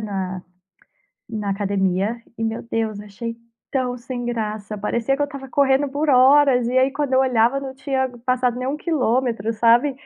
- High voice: Yes, high, 245 Hz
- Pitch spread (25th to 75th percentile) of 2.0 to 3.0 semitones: No, average, 3.5 semitones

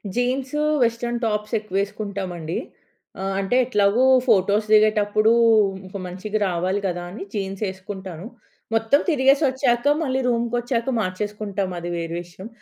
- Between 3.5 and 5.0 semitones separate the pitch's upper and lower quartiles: Yes, average, 3.8 semitones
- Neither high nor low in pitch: No, high, 210 Hz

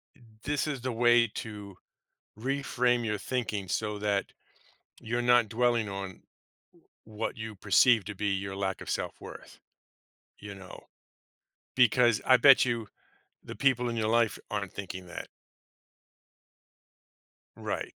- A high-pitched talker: No, low, 110 Hz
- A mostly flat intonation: No, average, 3.3 semitones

